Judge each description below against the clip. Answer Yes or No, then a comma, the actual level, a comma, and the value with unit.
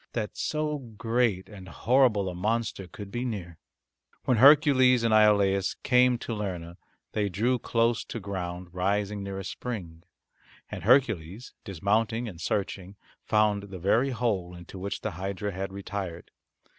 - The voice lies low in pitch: Yes, low, 105 Hz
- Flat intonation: No, average, 3.8 semitones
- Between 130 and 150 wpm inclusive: Yes, average, 145 wpm